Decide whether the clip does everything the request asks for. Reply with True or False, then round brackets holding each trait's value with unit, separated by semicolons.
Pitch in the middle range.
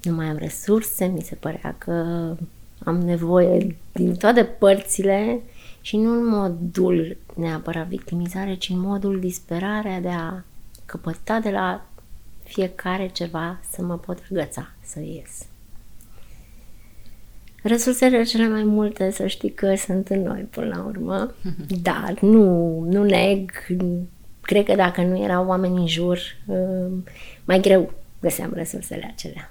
True (180 Hz)